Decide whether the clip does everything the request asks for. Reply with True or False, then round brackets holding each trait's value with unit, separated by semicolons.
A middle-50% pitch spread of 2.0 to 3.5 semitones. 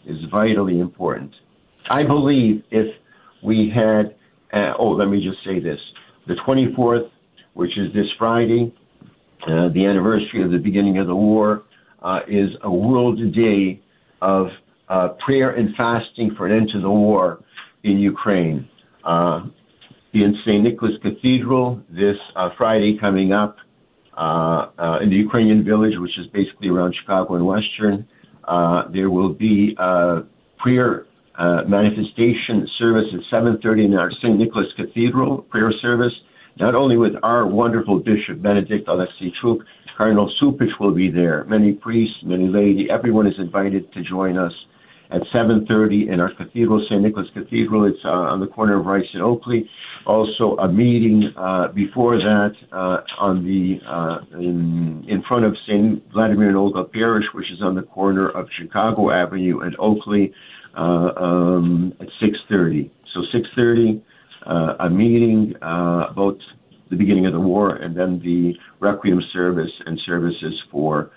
True (3.2 semitones)